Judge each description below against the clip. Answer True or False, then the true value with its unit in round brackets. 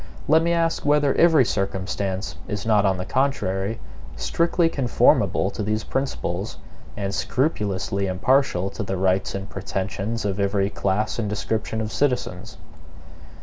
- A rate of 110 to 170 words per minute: True (140 wpm)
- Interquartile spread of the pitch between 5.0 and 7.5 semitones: True (5.4 semitones)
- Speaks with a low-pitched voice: True (105 Hz)